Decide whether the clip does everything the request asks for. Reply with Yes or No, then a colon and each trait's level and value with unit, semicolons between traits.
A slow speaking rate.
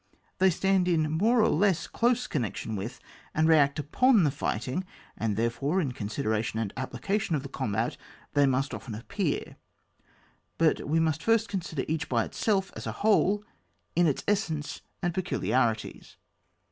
No: average, 160 wpm